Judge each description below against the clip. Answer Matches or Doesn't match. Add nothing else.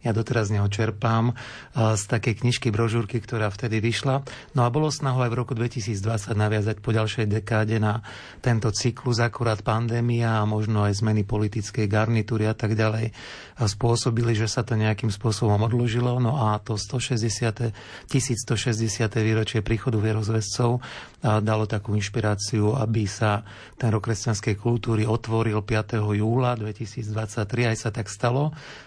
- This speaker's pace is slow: Doesn't match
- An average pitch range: Doesn't match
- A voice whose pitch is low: Matches